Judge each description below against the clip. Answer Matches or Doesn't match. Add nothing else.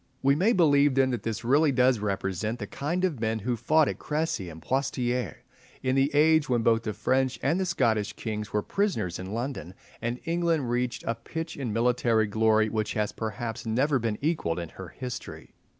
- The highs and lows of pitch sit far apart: Doesn't match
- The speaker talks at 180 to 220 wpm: Matches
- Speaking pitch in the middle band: Doesn't match